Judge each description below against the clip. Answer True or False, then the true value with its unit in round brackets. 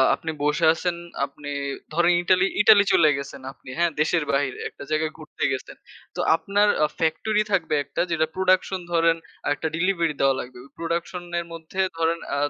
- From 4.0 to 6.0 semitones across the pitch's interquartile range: False (2.8 semitones)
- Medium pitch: True (165 Hz)